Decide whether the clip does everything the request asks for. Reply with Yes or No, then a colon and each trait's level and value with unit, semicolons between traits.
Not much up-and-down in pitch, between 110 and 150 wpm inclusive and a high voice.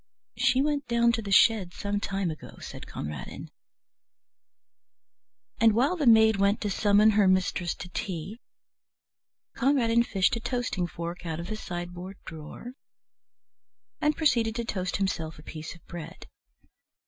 No: average, 4.8 semitones; average, 145 wpm; high, 200 Hz